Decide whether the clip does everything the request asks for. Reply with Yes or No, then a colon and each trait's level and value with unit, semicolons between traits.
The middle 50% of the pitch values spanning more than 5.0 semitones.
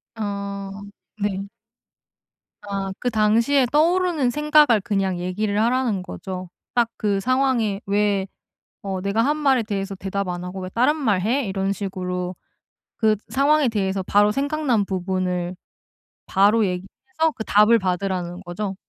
No: average, 4.2 semitones